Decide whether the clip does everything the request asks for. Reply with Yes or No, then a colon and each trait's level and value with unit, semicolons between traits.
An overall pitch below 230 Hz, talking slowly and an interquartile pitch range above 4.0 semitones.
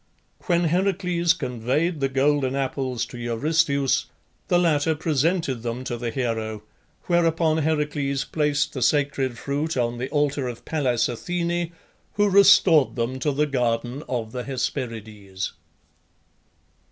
Yes: medium, 140 Hz; slow, 130 wpm; average, 4.7 semitones